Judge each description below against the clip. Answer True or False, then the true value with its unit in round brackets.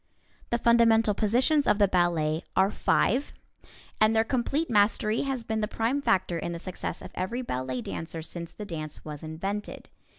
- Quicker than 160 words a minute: True (170 wpm)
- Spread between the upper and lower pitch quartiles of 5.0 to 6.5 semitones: True (5.6 semitones)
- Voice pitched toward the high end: True (210 Hz)